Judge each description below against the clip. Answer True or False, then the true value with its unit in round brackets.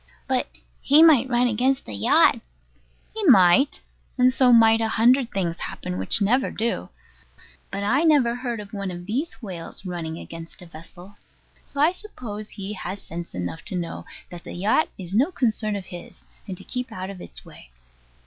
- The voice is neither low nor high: False (210 Hz)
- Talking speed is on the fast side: False (185 wpm)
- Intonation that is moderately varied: False (6.0 semitones)